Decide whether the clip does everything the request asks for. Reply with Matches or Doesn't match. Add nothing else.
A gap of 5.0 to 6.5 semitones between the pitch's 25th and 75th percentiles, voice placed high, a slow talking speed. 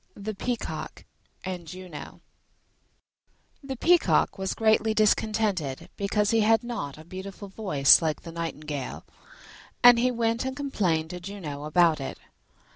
Matches